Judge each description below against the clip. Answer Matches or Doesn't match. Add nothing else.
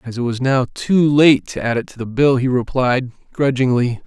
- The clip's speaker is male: Matches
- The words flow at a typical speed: Doesn't match